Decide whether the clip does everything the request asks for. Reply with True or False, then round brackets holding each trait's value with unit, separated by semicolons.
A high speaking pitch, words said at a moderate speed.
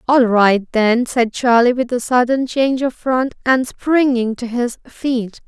True (245 Hz; 175 wpm)